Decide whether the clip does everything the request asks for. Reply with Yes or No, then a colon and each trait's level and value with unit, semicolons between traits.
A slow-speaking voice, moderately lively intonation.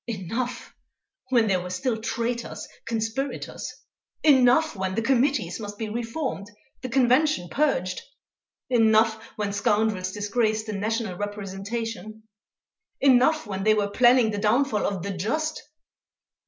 Yes: slow, 125 wpm; average, 3.4 semitones